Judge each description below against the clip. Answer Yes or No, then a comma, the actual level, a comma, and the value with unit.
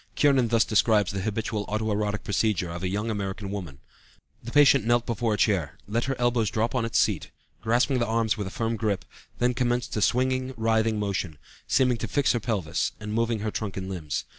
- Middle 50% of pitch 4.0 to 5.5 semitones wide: No, average, 2.7 semitones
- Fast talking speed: Yes, fast, 210 wpm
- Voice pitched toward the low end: Yes, low, 110 Hz